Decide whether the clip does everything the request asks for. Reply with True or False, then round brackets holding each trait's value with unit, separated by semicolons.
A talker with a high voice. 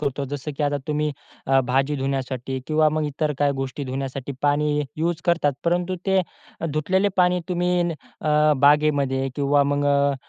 False (145 Hz)